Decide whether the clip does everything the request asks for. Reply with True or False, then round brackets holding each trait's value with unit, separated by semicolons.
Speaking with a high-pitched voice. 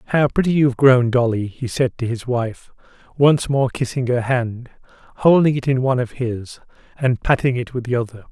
False (125 Hz)